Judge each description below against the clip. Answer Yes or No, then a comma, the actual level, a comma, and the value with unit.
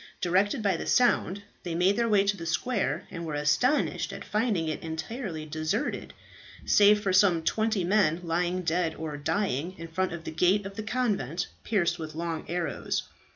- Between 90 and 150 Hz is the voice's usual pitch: No, medium, 180 Hz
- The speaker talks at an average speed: Yes, average, 180 wpm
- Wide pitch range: No, average, 4.1 semitones